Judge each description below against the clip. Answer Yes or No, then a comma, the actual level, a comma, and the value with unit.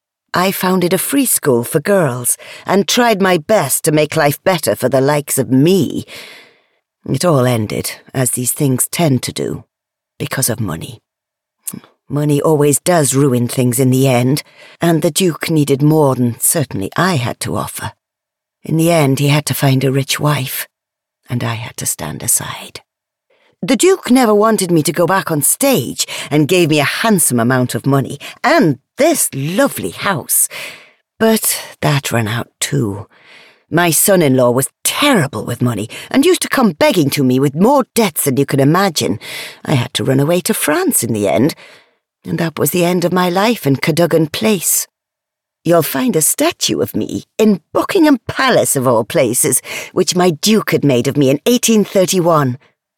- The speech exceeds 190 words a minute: No, average, 180 wpm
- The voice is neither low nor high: Yes, medium, 155 Hz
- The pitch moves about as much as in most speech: No, wide, 6.1 semitones